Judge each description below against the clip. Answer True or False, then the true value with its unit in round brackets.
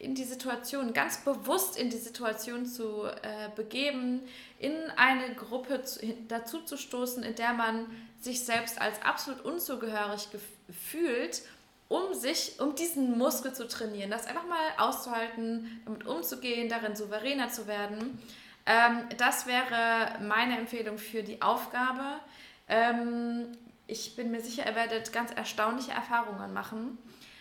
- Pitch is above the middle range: True (235 Hz)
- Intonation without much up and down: True (2.2 semitones)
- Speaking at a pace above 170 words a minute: False (130 wpm)